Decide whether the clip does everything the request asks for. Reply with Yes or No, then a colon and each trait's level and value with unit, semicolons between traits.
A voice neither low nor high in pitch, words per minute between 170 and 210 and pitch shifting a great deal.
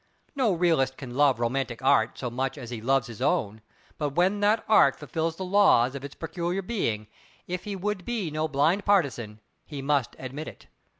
Yes: medium, 145 Hz; average, 190 wpm; wide, 5.9 semitones